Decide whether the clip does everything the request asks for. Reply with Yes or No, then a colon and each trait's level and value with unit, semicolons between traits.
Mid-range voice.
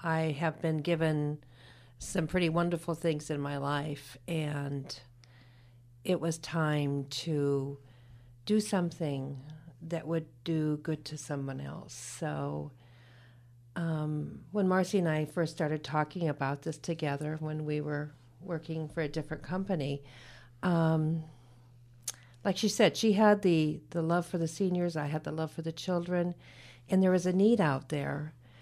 Yes: medium, 155 Hz